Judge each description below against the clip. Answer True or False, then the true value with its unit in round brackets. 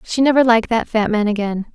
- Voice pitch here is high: True (225 Hz)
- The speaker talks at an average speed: False (240 wpm)